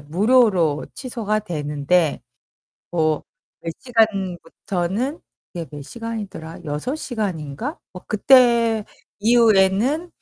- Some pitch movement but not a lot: No, wide, 6.2 semitones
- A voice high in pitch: Yes, high, 200 Hz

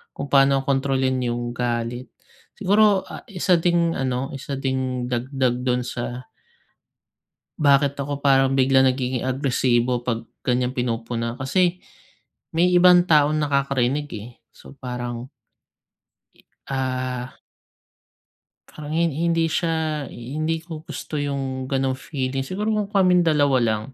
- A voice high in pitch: No, low, 135 Hz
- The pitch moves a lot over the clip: No, average, 3.5 semitones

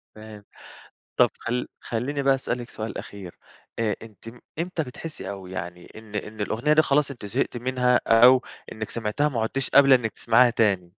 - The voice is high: No, low, 115 Hz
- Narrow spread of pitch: No, average, 3.6 semitones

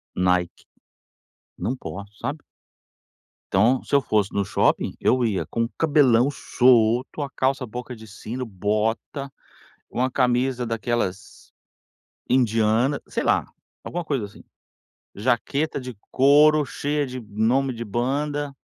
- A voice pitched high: No, low, 125 Hz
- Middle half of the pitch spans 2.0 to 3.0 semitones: No, average, 3.8 semitones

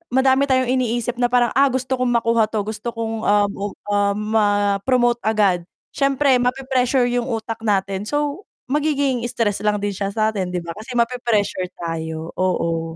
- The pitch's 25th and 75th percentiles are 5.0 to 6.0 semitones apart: No, average, 3.8 semitones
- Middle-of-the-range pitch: No, high, 225 Hz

